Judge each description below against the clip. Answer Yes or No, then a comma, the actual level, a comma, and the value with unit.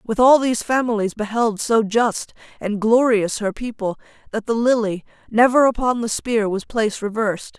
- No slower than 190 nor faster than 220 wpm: No, average, 165 wpm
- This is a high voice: Yes, high, 225 Hz